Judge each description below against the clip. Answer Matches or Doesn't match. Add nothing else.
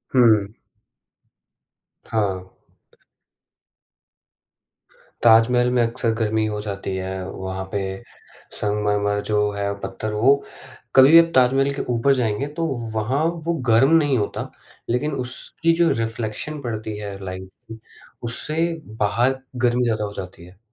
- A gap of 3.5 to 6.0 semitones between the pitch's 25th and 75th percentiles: Matches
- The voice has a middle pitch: Doesn't match